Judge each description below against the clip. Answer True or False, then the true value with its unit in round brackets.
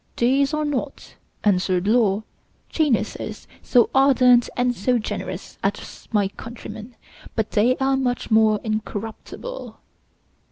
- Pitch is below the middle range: False (240 Hz)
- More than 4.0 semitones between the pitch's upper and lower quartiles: False (3.7 semitones)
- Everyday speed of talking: False (115 wpm)